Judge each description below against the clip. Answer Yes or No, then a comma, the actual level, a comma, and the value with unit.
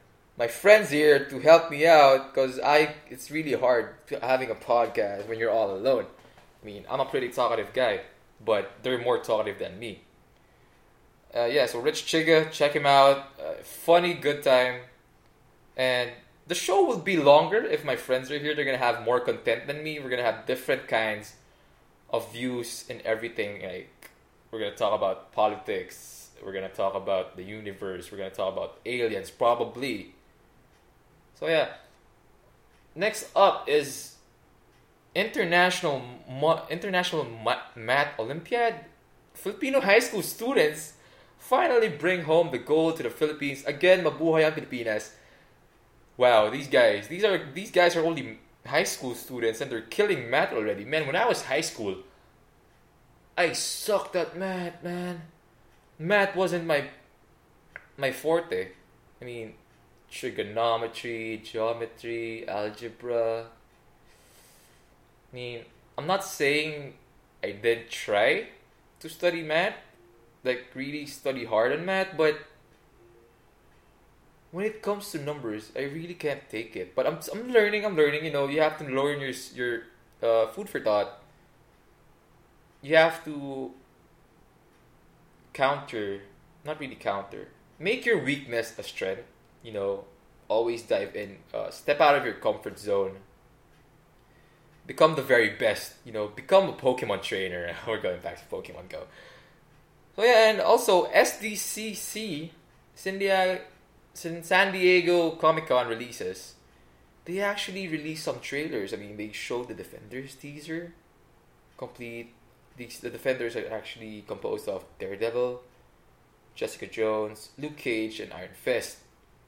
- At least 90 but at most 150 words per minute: Yes, average, 140 wpm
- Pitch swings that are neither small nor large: No, wide, 6.5 semitones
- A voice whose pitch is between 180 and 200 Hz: No, medium, 140 Hz